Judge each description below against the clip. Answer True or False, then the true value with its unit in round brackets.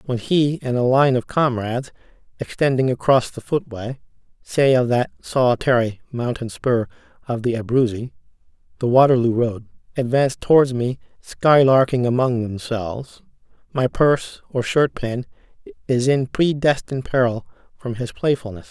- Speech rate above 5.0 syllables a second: False (4.8 syllables/s)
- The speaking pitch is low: True (125 Hz)